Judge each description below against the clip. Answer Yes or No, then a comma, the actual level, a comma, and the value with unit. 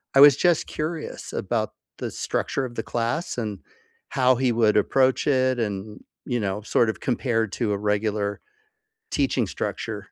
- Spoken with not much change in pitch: No, average, 3.6 semitones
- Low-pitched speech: Yes, low, 120 Hz